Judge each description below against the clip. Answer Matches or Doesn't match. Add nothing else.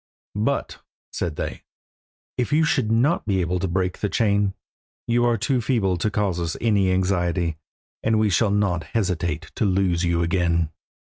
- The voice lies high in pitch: Doesn't match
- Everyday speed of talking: Matches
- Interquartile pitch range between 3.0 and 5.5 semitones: Matches